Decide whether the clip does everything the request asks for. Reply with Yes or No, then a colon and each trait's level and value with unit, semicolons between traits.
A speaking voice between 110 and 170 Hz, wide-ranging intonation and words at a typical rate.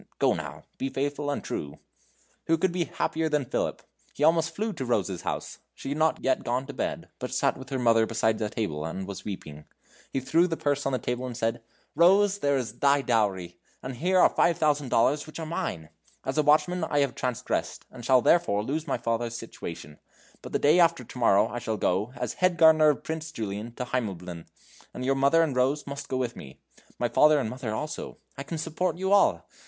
No: low, 135 Hz; wide, 5.7 semitones; fast, 220 wpm